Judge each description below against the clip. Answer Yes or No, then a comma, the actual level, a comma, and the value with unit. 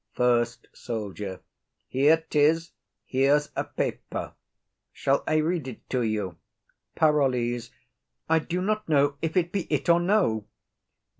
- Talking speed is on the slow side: Yes, slow, 130 wpm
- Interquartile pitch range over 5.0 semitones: Yes, wide, 5.4 semitones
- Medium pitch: Yes, medium, 145 Hz